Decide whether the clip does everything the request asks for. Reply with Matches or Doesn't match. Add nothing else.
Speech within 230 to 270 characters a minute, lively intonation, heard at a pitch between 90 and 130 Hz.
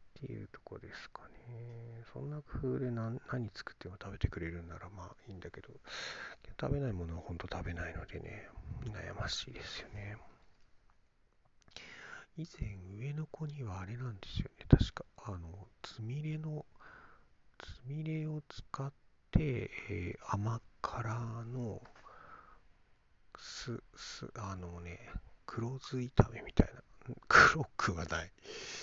Matches